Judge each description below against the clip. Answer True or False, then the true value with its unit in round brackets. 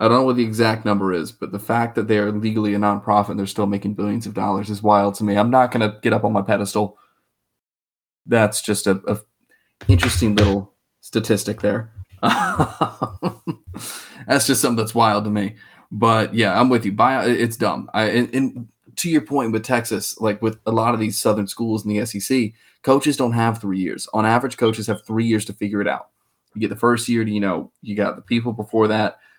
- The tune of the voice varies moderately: False (2.2 semitones)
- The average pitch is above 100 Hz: True (110 Hz)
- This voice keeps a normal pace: False (220 wpm)